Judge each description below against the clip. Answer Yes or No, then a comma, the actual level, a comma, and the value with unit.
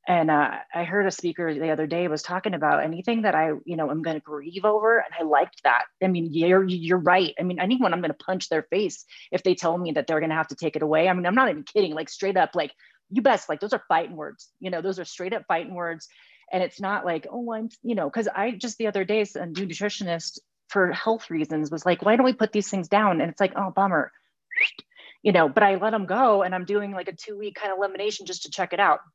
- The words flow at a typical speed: No, fast, 275 wpm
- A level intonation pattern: No, average, 3.9 semitones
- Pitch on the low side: No, medium, 185 Hz